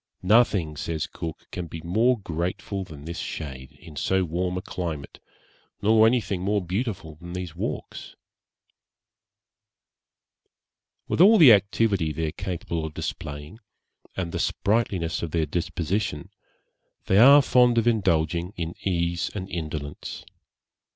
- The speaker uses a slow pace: Yes, slow, 130 wpm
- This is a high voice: No, very low, 90 Hz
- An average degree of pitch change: Yes, average, 4.3 semitones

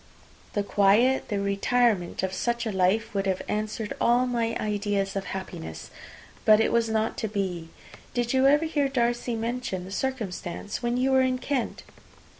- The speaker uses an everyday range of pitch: Yes, average, 3.7 semitones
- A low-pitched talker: No, high, 220 Hz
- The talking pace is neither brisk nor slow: Yes, average, 170 wpm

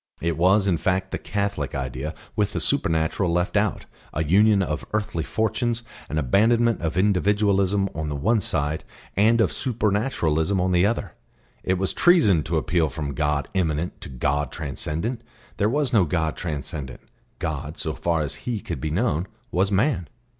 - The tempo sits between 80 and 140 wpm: No, average, 170 wpm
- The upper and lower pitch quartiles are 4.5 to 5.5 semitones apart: Yes, average, 5.1 semitones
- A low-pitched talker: Yes, very low, 90 Hz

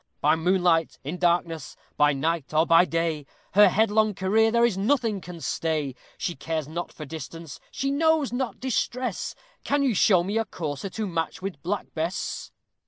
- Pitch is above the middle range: No, medium, 180 Hz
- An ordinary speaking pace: Yes, average, 170 wpm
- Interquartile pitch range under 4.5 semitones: No, average, 5.2 semitones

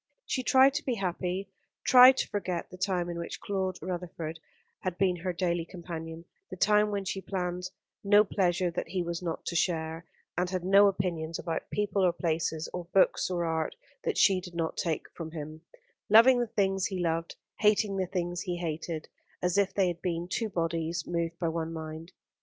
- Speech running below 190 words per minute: No, average, 195 wpm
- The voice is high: No, medium, 180 Hz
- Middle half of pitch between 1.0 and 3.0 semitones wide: Yes, narrow, 2.6 semitones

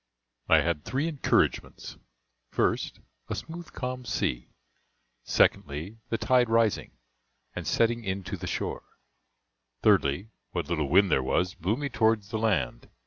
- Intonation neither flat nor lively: No, wide, 5.7 semitones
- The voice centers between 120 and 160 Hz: No, low, 105 Hz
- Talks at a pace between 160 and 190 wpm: No, average, 140 wpm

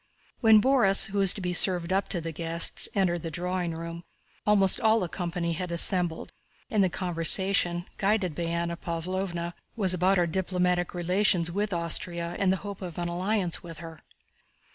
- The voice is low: No, medium, 180 Hz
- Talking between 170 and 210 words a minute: Yes, average, 175 wpm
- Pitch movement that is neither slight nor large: No, narrow, 2.3 semitones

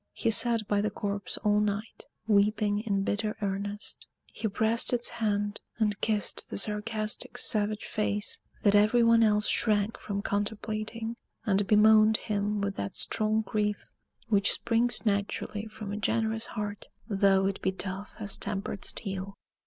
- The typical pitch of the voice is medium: No, high, 210 Hz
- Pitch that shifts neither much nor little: No, narrow, 1.4 semitones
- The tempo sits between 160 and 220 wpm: No, average, 150 wpm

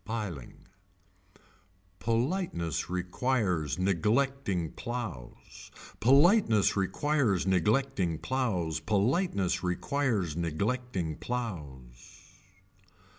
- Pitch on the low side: Yes, low, 100 Hz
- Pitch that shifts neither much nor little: No, wide, 6.7 semitones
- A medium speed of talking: No, slow, 60 wpm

